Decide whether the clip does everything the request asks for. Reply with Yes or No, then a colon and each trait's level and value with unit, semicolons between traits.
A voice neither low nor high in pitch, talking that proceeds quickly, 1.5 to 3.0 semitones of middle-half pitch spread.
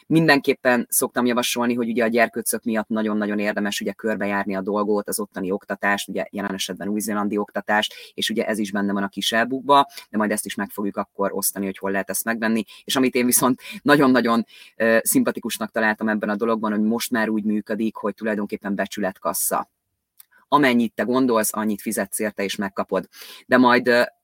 No: low, 110 Hz; fast, 180 wpm; average, 2.7 semitones